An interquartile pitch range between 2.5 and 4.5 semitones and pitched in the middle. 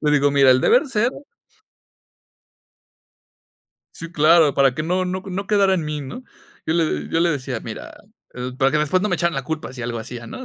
No: average, 5.0 semitones; medium, 155 Hz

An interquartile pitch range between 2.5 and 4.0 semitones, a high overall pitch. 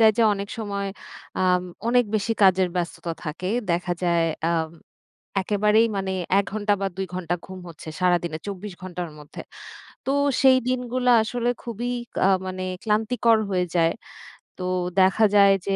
Yes: average, 3.6 semitones; high, 195 Hz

